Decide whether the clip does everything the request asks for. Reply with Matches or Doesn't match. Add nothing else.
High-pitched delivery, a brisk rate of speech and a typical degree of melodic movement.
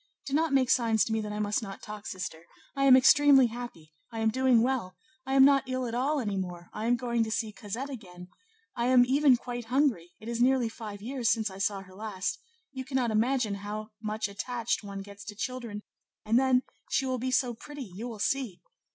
Matches